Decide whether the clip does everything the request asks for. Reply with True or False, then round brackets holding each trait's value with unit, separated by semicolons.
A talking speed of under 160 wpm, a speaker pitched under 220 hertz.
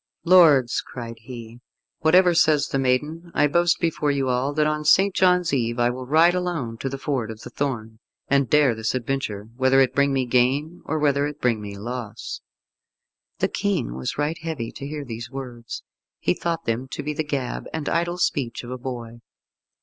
False (195 wpm; 135 Hz)